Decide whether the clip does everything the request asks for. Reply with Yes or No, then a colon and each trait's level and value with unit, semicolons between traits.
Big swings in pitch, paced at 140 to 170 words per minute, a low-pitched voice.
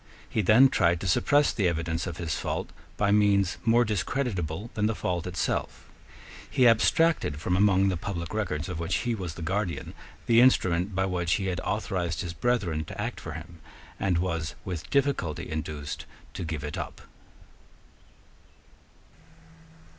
No: average, 4.2 semitones; average, 160 wpm; very low, 90 Hz